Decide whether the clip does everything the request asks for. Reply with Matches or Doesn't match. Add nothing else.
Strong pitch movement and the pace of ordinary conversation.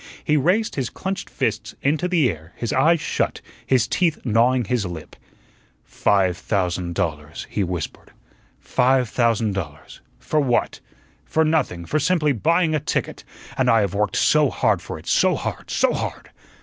Matches